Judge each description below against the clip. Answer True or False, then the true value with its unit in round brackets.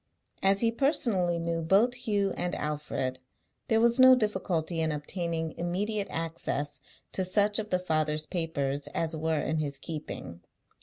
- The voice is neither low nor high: True (170 Hz)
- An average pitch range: True (4.8 semitones)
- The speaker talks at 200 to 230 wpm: False (150 wpm)